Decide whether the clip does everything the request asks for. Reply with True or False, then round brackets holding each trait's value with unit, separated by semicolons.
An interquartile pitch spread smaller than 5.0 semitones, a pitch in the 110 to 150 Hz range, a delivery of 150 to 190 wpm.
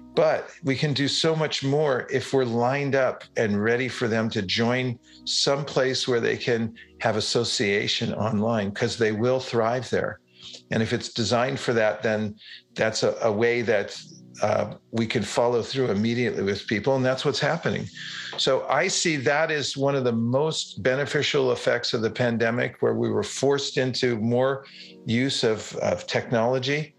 True (3.0 semitones; 125 Hz; 175 wpm)